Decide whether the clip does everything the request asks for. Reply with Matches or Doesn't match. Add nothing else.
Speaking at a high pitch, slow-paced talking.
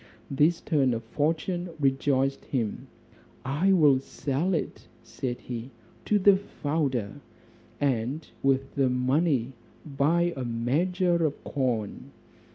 Doesn't match